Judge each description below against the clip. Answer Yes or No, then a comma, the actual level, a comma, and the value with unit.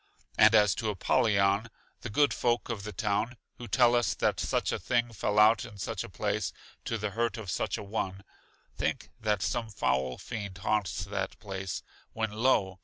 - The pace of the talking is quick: No, average, 185 wpm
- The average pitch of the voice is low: Yes, low, 105 Hz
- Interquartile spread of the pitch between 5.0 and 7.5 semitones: No, average, 2.8 semitones